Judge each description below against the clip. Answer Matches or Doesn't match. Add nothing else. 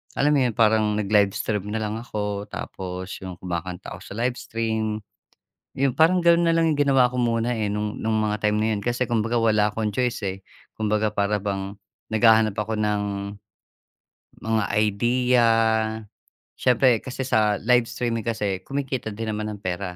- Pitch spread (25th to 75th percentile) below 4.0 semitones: Matches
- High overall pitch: Doesn't match